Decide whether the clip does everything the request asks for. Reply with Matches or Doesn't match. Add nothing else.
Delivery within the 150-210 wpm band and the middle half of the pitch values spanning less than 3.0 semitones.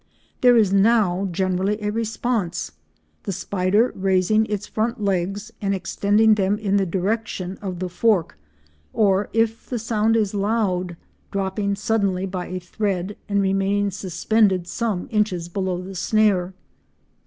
Doesn't match